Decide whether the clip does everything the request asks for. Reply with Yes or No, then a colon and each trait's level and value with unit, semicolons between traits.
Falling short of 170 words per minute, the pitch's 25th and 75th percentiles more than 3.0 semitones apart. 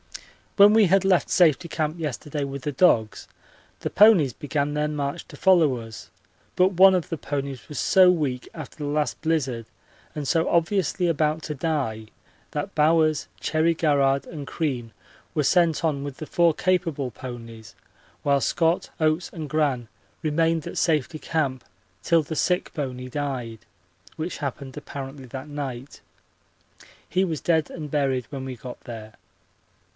Yes: average, 155 wpm; average, 3.5 semitones